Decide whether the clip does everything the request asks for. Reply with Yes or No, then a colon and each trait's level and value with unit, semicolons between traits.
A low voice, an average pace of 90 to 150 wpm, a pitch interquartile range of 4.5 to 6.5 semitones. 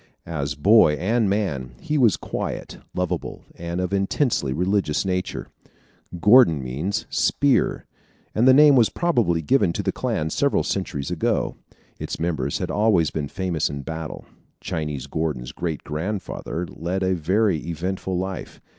Yes: very low, 90 Hz; average, 145 wpm; average, 4.8 semitones